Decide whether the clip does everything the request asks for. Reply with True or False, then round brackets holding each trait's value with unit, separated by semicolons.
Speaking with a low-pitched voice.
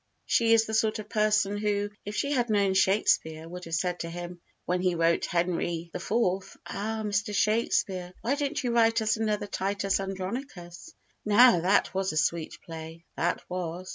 False (195 Hz)